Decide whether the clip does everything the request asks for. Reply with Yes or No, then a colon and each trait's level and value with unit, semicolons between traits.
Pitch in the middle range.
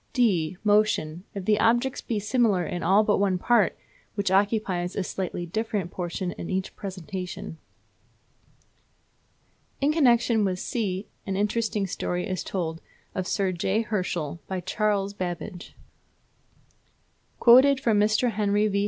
No: high, 200 Hz